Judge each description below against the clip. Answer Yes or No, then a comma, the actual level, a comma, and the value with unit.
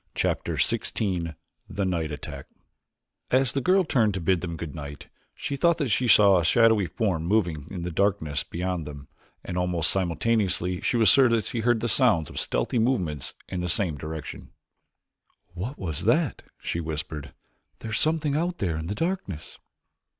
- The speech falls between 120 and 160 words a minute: No, average, 175 wpm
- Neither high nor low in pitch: No, very low, 95 Hz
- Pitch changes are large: Yes, wide, 6.2 semitones